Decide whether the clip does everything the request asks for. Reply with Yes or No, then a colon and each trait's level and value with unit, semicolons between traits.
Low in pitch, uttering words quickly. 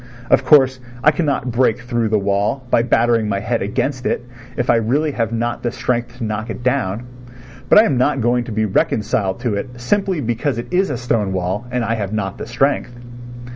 Yes: low, 120 Hz; fast, 210 wpm